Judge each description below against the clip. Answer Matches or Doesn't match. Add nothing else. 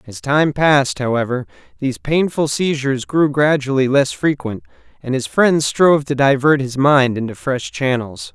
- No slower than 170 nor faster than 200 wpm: Doesn't match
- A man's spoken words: Matches